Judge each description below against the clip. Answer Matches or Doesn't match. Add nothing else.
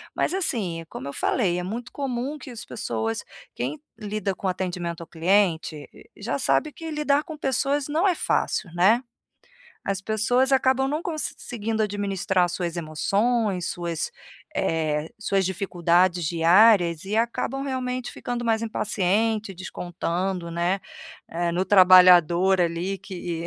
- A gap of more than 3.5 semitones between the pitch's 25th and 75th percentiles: Matches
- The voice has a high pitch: Matches